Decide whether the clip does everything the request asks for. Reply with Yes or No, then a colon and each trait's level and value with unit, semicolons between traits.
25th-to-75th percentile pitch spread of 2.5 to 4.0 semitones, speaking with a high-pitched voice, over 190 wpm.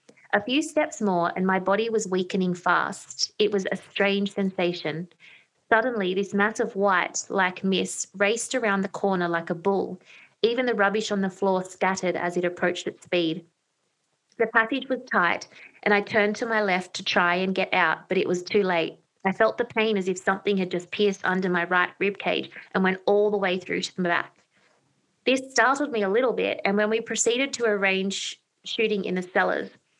Yes: average, 3.1 semitones; high, 195 Hz; average, 200 wpm